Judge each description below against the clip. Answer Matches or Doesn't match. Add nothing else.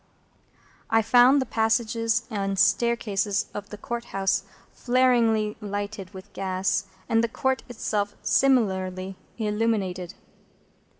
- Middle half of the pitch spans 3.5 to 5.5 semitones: Doesn't match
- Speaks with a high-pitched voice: Matches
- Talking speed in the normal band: Doesn't match